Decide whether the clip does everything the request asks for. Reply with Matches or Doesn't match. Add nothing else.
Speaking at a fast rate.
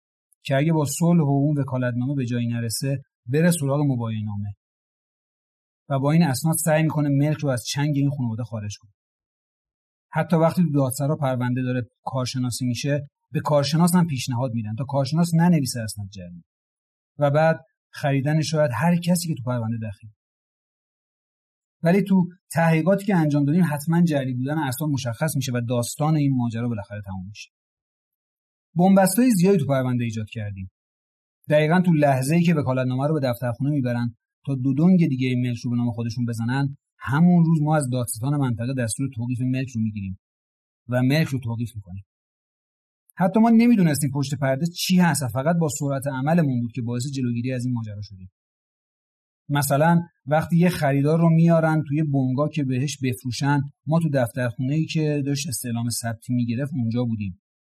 Matches